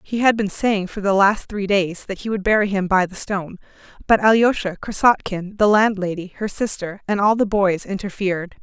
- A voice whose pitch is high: Yes, high, 200 Hz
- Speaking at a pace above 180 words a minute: Yes, average, 200 wpm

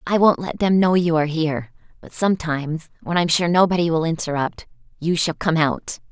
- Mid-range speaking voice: Yes, medium, 165 Hz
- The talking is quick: No, average, 195 wpm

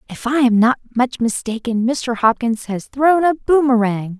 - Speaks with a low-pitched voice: No, high, 245 Hz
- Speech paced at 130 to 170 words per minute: Yes, average, 155 wpm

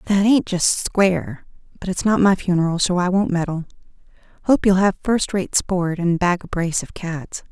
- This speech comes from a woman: Yes, female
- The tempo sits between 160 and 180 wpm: No, average, 200 wpm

